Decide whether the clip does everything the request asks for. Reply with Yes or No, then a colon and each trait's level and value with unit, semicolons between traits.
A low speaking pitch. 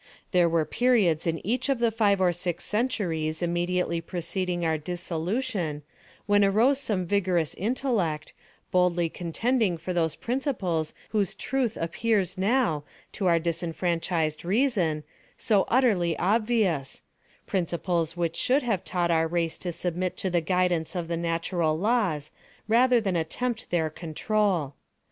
No: medium, 180 Hz